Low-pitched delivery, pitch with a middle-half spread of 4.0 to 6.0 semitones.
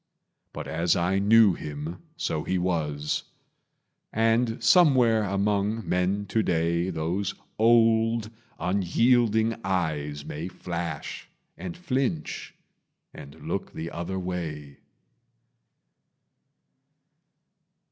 Yes: very low, 95 Hz; average, 5.1 semitones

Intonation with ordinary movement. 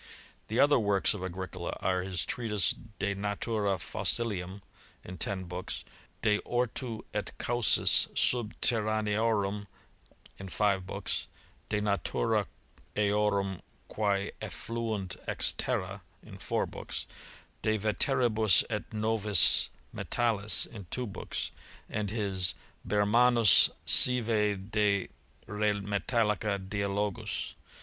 No: narrow, 2.0 semitones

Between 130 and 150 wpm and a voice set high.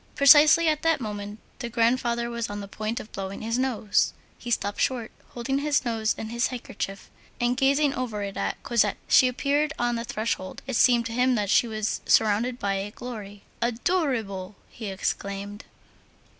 No: average, 175 wpm; high, 235 Hz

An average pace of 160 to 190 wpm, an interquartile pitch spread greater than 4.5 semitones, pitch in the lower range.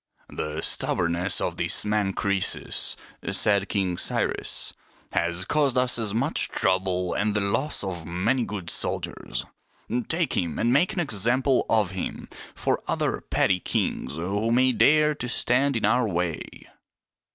No: average, 150 wpm; wide, 5.5 semitones; low, 105 Hz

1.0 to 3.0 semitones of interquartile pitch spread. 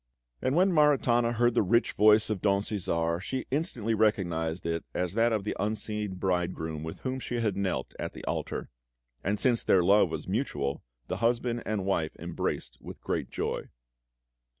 No: average, 5.0 semitones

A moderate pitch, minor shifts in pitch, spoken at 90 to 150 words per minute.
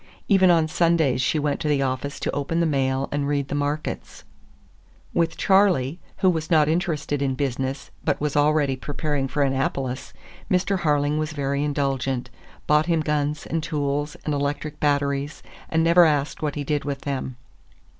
No: medium, 145 Hz; narrow, 2.1 semitones; average, 170 wpm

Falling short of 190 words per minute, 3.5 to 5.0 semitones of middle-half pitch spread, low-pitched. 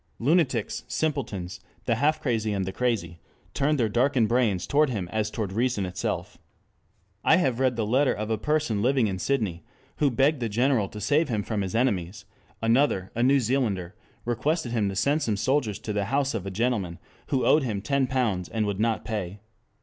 No: average, 195 wpm; average, 4.7 semitones; low, 115 Hz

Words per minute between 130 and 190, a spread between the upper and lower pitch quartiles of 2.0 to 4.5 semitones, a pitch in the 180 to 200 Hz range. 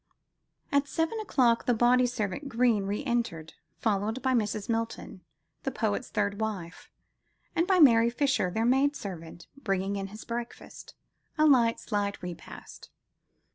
No: average, 140 wpm; average, 4.2 semitones; high, 230 Hz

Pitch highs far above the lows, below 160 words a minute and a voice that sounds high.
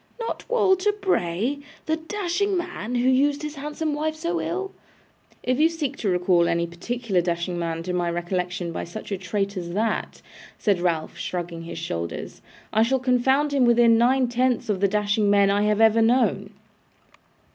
No: wide, 8.3 semitones; average, 175 wpm; high, 225 Hz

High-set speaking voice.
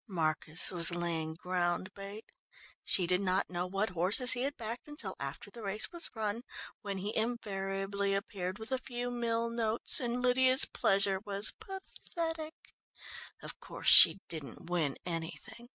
Yes: high, 200 Hz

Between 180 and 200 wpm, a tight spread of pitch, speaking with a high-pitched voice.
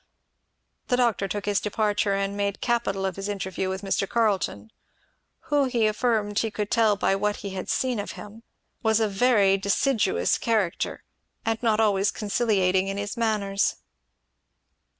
No: average, 155 wpm; narrow, 2.3 semitones; high, 205 Hz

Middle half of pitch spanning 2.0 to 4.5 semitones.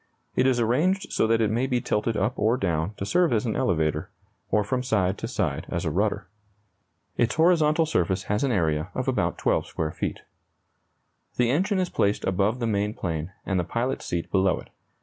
No: average, 5.2 semitones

